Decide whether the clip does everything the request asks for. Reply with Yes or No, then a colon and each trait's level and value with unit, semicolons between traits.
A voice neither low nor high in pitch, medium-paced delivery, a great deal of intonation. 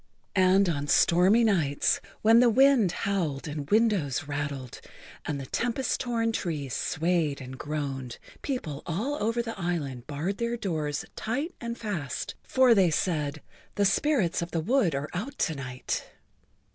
Yes: medium, 175 Hz; average, 150 wpm; wide, 7.8 semitones